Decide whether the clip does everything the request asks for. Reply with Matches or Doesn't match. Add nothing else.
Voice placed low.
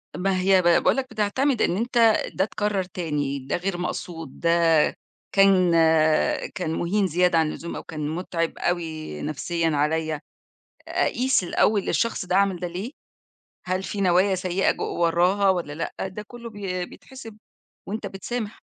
Doesn't match